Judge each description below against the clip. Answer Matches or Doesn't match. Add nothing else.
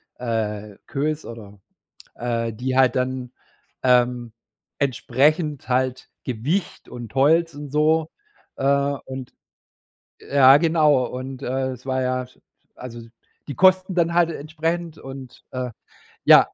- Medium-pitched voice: Doesn't match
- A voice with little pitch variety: Doesn't match